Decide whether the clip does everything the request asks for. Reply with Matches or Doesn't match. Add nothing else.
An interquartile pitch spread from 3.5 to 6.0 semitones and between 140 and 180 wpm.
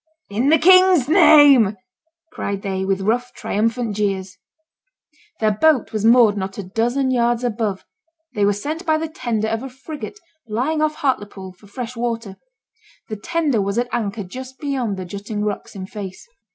Matches